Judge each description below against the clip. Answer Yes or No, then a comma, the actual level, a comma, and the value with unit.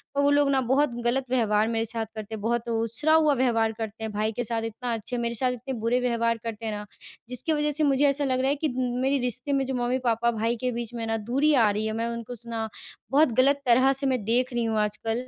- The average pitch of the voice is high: Yes, high, 240 Hz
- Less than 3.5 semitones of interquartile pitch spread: Yes, average, 2.9 semitones